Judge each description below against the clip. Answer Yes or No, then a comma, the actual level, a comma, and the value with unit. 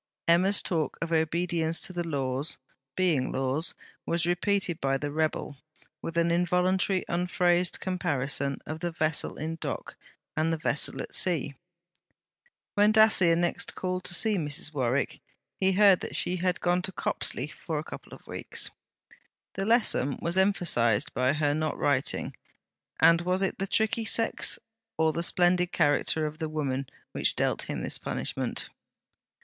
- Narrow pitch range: No, average, 3.3 semitones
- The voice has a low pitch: No, medium, 170 Hz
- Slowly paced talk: No, average, 155 wpm